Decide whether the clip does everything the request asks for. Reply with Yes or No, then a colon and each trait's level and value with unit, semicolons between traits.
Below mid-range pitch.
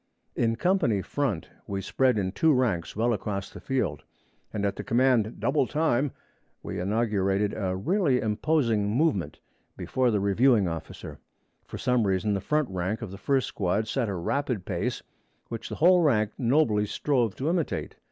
Yes: low, 115 Hz